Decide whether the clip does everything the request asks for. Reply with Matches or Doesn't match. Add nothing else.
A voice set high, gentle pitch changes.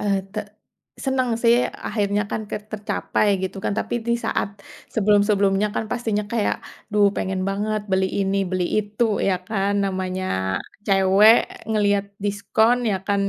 Matches